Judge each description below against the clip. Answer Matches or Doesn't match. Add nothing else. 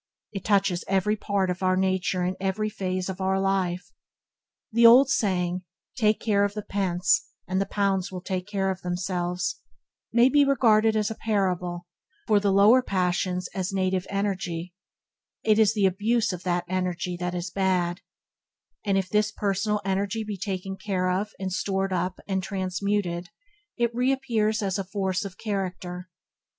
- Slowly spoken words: Doesn't match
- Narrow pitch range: Matches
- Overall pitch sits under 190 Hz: Doesn't match